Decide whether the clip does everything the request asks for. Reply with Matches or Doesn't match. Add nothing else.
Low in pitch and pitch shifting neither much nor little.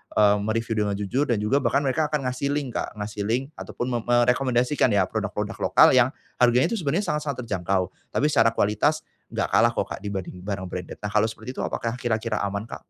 Matches